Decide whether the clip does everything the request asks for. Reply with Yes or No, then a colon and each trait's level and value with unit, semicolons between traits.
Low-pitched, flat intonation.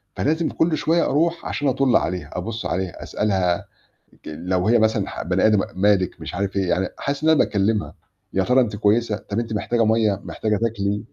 No: low, 105 Hz; average, 3.7 semitones